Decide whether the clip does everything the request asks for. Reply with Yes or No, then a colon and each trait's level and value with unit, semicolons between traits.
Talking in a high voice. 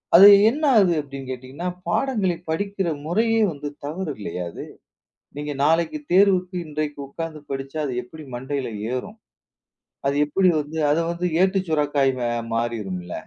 No: medium, 155 Hz